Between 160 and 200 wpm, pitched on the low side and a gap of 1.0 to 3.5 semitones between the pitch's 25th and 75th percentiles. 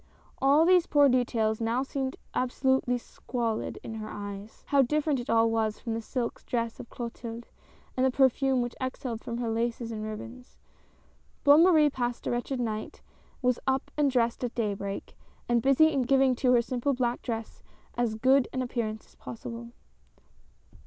No: average, 170 wpm; high, 245 Hz; narrow, 2.6 semitones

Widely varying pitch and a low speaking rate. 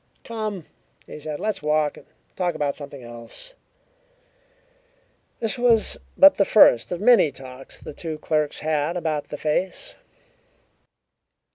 Yes: wide, 6.3 semitones; slow, 130 wpm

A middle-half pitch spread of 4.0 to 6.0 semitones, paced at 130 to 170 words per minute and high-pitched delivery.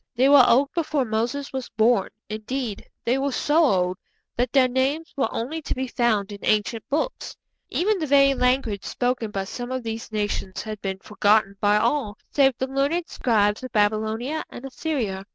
No: average, 4.4 semitones; average, 180 wpm; high, 245 Hz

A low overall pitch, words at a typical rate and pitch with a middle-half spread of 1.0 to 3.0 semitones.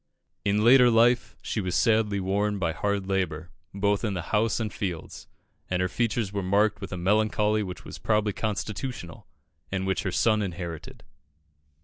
Yes: low, 100 Hz; average, 165 wpm; average, 2.7 semitones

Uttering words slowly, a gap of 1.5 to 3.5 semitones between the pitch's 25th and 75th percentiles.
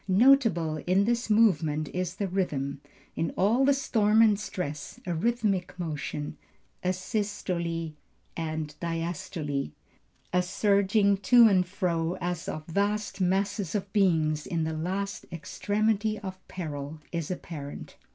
No: slow, 130 wpm; average, 4.1 semitones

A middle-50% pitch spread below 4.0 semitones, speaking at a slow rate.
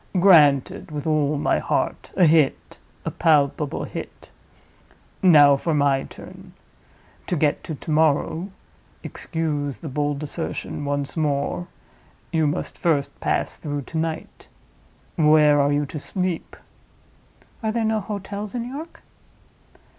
Yes: average, 3.3 semitones; slow, 125 wpm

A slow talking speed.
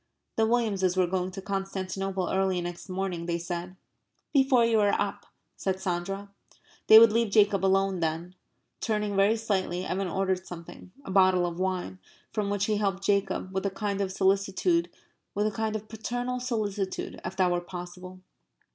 No: average, 170 wpm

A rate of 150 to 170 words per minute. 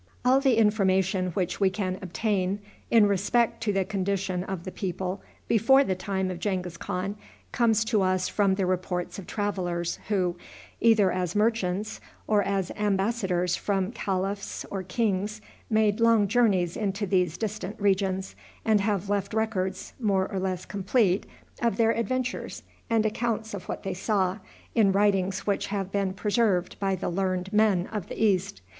Yes: average, 160 wpm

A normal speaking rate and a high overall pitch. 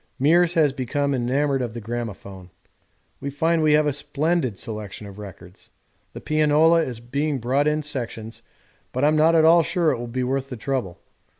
No: average, 185 wpm; low, 135 Hz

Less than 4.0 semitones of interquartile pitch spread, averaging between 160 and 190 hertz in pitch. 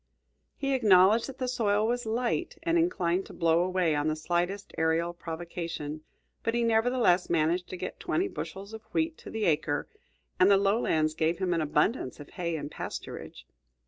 No: wide, 5.6 semitones; medium, 185 Hz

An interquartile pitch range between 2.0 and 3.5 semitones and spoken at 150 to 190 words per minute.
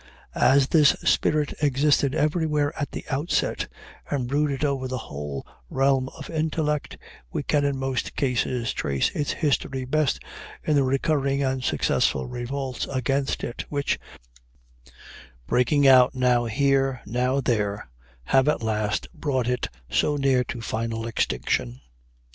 No: average, 2.8 semitones; slow, 135 wpm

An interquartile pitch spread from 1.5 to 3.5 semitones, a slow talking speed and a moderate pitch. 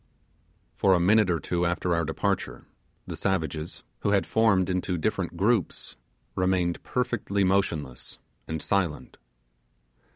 No: average, 2.8 semitones; slow, 125 wpm; very low, 90 Hz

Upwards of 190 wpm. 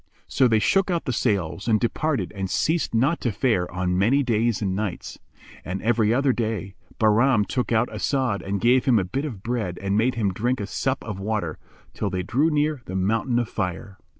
Yes: fast, 205 wpm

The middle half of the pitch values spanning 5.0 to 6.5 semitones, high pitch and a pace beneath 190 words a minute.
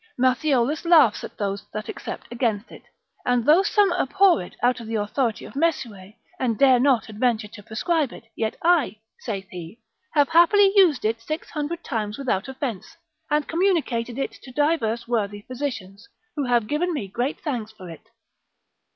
Yes: wide, 5.6 semitones; high, 245 Hz; average, 170 wpm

